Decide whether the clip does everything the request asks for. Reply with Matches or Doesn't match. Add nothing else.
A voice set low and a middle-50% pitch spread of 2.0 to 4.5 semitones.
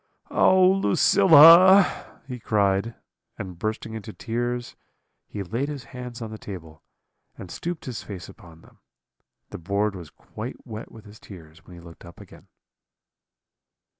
Doesn't match